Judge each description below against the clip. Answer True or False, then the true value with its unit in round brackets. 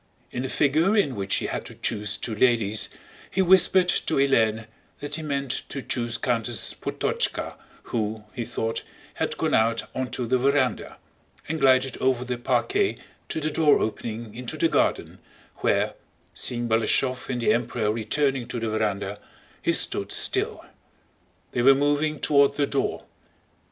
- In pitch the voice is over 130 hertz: False (125 Hz)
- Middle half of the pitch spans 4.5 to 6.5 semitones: False (3.9 semitones)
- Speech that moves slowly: False (155 wpm)